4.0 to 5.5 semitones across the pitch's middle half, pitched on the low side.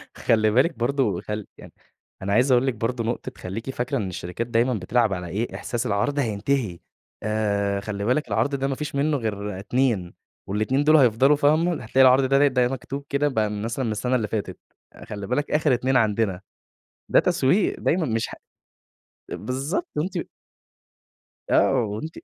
Yes: average, 4.6 semitones; low, 120 Hz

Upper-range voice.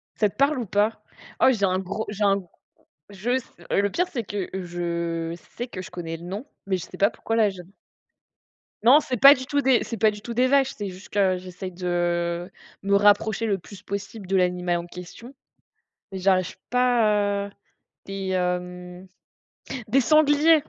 Yes: high, 200 Hz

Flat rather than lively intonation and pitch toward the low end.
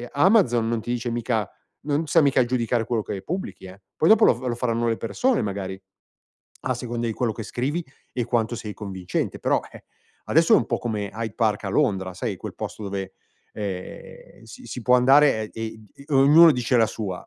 No: average, 3.5 semitones; low, 115 Hz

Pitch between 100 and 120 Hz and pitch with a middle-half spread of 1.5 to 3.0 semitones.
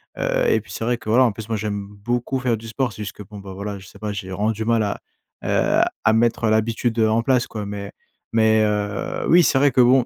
Yes: low, 110 Hz; average, 2.7 semitones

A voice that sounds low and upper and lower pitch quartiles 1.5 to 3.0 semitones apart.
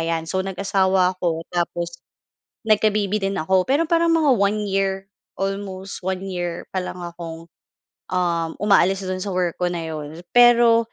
No: high, 190 Hz; average, 2.7 semitones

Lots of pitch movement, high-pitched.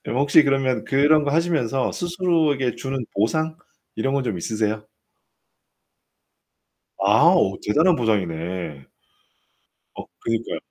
No: wide, 6.4 semitones; low, 130 Hz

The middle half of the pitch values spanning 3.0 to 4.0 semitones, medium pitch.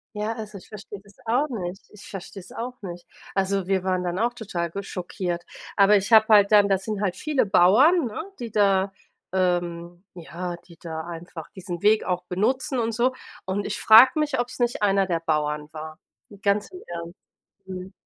No: average, 3.7 semitones; high, 195 Hz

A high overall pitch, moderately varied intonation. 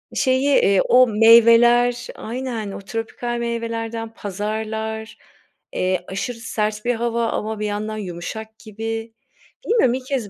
No: high, 225 Hz; narrow, 1.8 semitones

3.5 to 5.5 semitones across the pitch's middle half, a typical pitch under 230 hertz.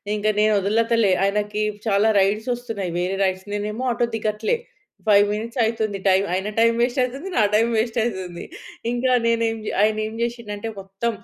No: narrow, 2.5 semitones; high, 215 Hz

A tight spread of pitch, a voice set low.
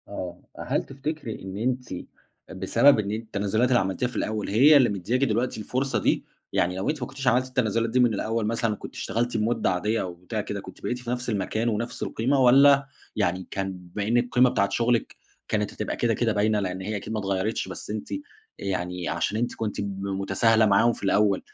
No: average, 3.8 semitones; low, 110 Hz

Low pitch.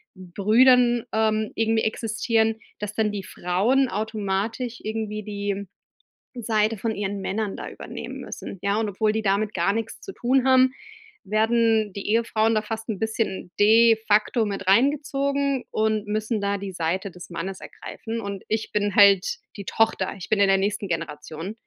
No: high, 215 Hz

